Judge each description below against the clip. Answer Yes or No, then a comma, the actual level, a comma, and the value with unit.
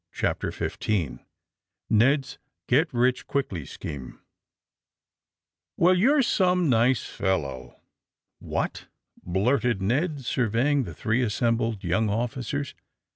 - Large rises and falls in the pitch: Yes, wide, 5.7 semitones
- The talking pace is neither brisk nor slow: No, slow, 95 wpm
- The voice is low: Yes, low, 120 Hz